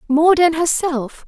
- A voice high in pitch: Yes, very high, 310 Hz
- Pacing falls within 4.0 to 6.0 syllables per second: No, 3.7 syllables/s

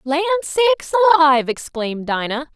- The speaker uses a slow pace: Yes, slow, 115 wpm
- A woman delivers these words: Yes, female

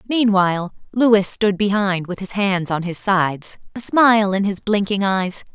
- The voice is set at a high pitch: Yes, high, 200 Hz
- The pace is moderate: Yes, average, 175 wpm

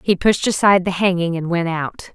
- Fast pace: Yes, fast, 225 wpm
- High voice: No, medium, 180 Hz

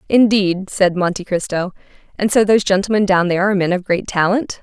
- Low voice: No, high, 190 Hz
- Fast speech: No, average, 195 wpm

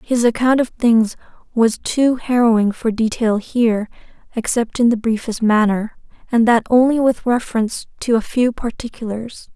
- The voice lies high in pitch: Yes, high, 230 Hz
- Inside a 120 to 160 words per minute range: Yes, average, 150 wpm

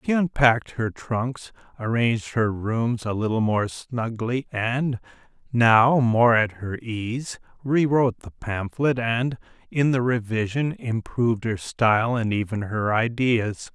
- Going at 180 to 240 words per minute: No, slow, 135 wpm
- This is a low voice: Yes, low, 120 Hz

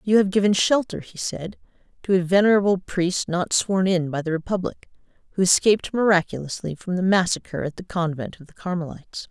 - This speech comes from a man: No, female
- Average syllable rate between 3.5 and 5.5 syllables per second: No, 5.7 syllables/s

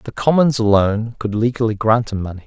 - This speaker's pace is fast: No, average, 195 wpm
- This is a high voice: No, low, 115 Hz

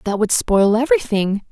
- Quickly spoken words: No, average, 160 wpm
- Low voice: No, high, 205 Hz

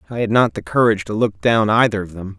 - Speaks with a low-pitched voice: Yes, low, 105 Hz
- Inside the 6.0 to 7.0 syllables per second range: Yes, 6.4 syllables/s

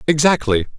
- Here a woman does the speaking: No, male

